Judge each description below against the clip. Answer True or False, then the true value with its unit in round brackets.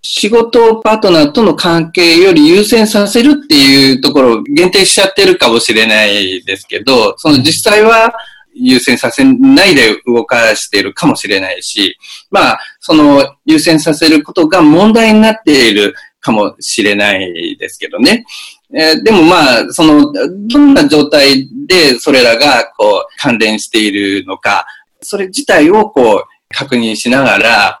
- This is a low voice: False (230 Hz)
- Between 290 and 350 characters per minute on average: True (300 characters per minute)